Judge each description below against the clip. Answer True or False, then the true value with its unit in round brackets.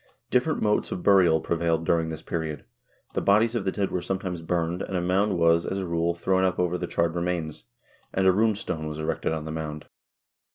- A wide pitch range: False (2.7 semitones)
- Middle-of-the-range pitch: False (85 Hz)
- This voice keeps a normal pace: False (215 wpm)